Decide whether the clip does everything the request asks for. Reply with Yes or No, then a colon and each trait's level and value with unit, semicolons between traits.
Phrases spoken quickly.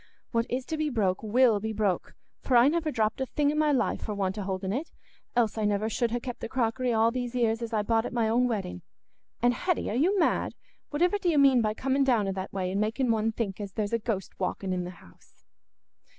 Yes: fast, 250 wpm